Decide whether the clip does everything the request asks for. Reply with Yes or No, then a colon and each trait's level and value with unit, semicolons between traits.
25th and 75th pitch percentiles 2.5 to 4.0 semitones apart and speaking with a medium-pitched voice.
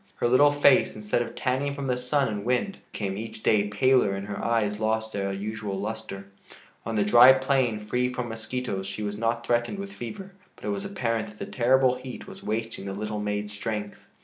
No: average, 3.5 semitones; low, 115 Hz